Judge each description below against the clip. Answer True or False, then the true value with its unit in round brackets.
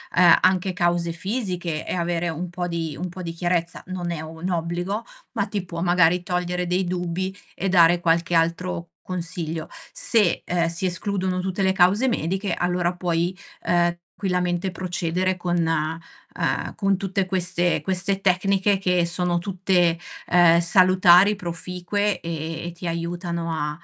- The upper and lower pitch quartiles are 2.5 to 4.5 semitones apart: False (1.7 semitones)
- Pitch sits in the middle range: True (175 Hz)